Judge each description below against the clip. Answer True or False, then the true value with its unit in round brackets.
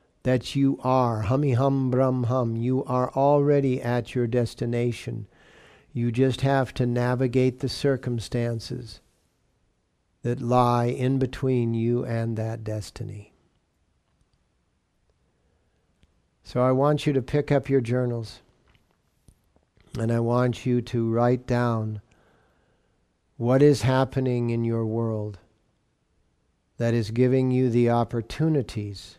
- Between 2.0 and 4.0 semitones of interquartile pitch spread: True (2.5 semitones)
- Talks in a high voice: False (120 Hz)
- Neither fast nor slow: False (115 wpm)